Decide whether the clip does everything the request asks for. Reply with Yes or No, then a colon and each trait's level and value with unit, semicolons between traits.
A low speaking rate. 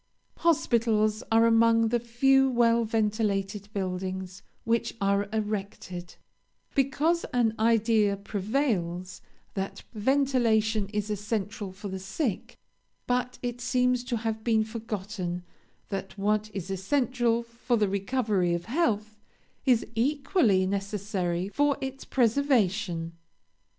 Yes: slow, 110 wpm